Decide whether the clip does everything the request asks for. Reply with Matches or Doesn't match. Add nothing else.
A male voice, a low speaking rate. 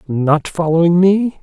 Matches